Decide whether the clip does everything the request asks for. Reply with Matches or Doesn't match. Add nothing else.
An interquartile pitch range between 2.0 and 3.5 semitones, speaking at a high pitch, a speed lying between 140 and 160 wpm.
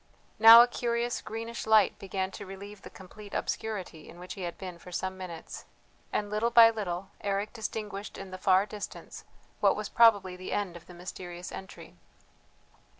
Doesn't match